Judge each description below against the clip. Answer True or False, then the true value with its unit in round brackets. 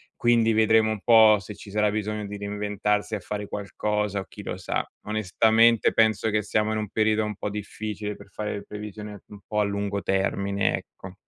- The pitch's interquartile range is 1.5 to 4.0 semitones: False (1.1 semitones)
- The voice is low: True (105 Hz)